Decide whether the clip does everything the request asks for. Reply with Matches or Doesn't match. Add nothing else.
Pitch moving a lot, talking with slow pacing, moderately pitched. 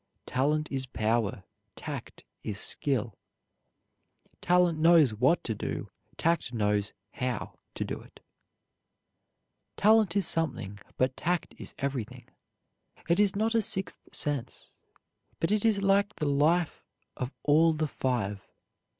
Matches